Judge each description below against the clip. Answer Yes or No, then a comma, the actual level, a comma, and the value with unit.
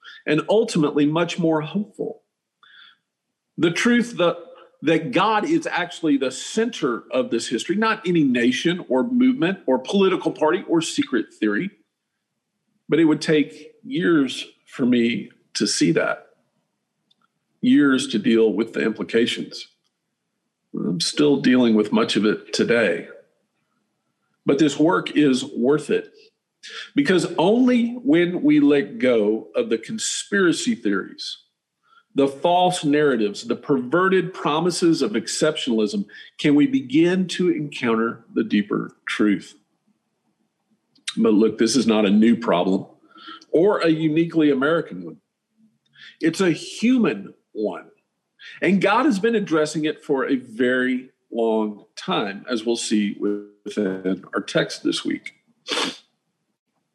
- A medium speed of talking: No, slow, 125 wpm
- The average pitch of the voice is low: No, medium, 165 Hz